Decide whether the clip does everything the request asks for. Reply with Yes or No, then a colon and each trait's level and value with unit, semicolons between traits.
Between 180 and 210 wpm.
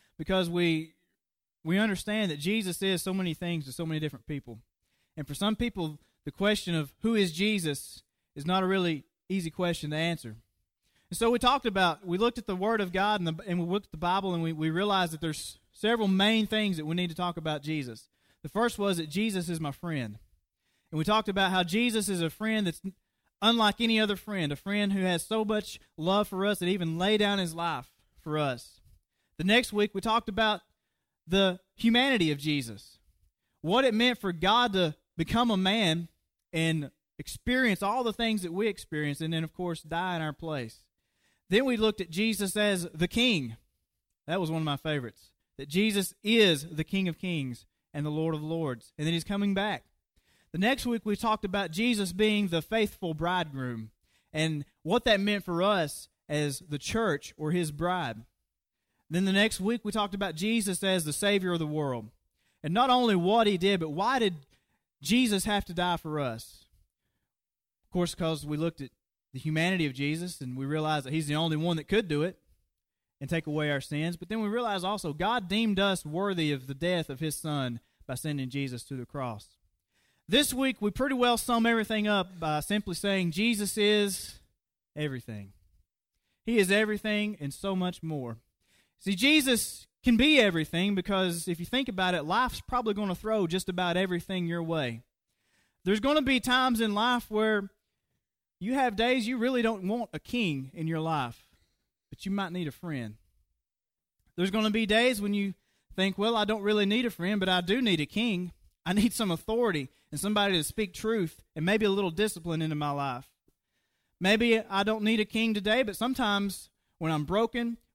Yes: average, 200 wpm